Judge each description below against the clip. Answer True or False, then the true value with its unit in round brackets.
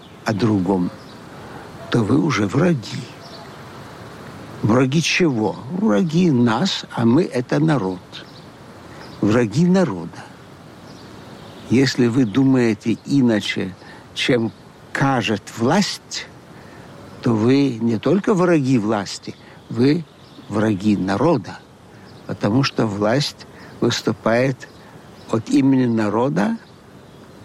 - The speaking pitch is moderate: False (125 Hz)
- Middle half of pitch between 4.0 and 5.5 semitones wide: True (4.9 semitones)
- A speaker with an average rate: False (85 wpm)